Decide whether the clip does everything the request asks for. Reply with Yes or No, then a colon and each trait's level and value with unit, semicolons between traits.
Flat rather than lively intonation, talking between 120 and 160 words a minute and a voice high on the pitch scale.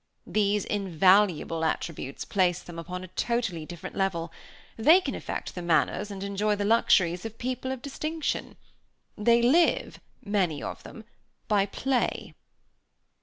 No: average, 4.9 semitones; slow, 135 wpm; high, 200 Hz